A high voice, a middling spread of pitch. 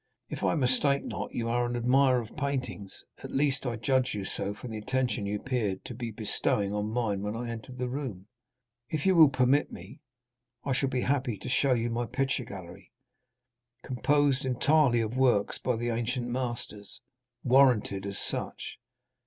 No: low, 125 Hz; average, 3.2 semitones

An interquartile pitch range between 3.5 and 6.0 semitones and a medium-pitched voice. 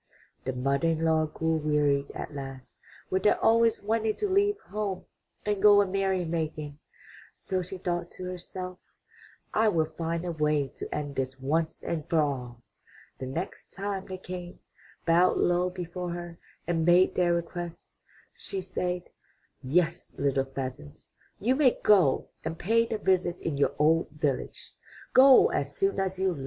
Yes: average, 3.9 semitones; medium, 175 Hz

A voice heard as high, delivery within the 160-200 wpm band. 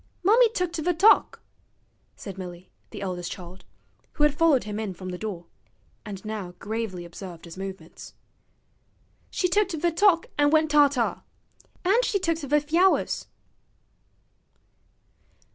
No: very high, 265 Hz; average, 140 wpm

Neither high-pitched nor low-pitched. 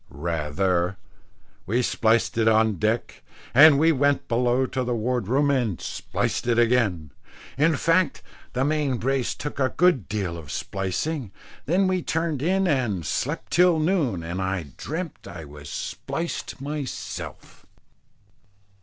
No: low, 125 Hz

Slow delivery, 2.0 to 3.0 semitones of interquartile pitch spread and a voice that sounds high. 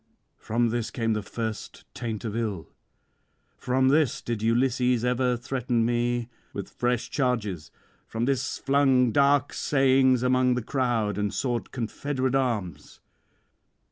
No: slow, 130 wpm; narrow, 2.4 semitones; low, 120 Hz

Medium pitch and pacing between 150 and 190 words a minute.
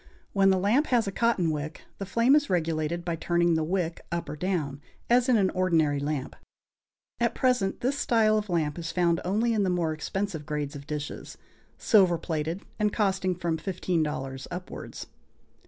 Yes: medium, 175 Hz; average, 175 wpm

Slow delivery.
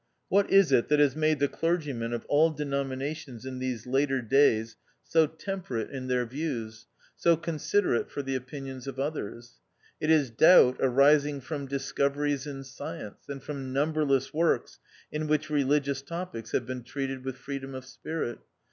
No: average, 165 wpm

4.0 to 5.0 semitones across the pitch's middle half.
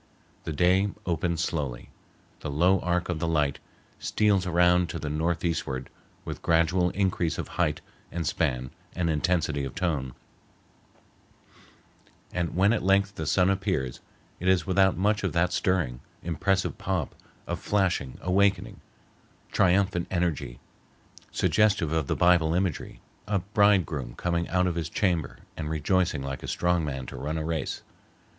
No: average, 3.2 semitones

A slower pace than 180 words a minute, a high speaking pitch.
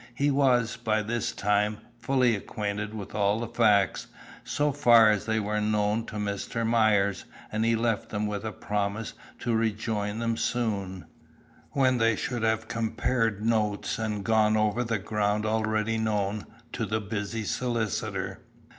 No: average, 155 wpm; low, 110 Hz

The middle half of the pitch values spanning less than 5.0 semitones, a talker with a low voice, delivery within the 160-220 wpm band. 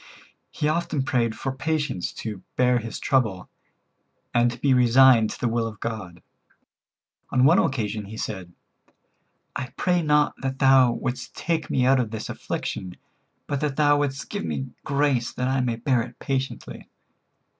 Yes: average, 3.2 semitones; low, 130 Hz; average, 165 wpm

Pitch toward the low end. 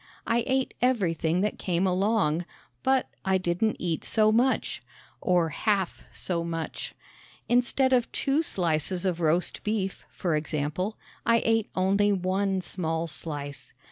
No: medium, 185 Hz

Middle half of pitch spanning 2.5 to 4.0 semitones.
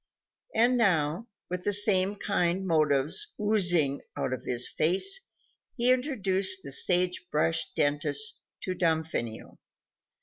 No: average, 4.9 semitones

